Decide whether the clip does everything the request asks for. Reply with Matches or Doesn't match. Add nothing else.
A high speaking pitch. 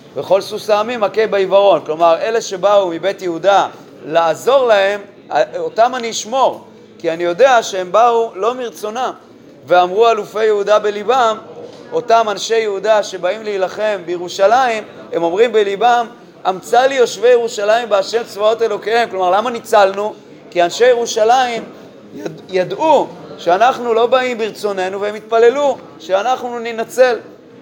Matches